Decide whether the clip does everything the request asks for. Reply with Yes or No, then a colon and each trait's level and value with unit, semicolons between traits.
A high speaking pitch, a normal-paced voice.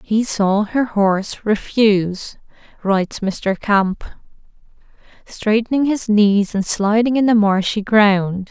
No: high, 210 Hz; slow, 120 wpm